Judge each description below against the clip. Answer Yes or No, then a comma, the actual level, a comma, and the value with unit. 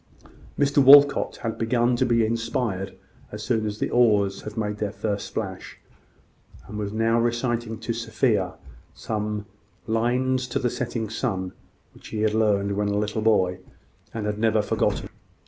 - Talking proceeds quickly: No, average, 160 wpm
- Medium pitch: No, low, 110 Hz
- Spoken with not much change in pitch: Yes, narrow, 2.3 semitones